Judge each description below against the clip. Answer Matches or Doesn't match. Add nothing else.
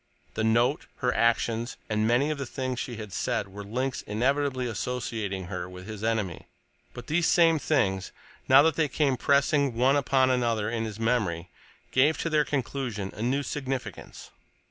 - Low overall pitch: Matches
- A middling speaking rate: Matches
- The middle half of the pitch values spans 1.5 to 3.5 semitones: Doesn't match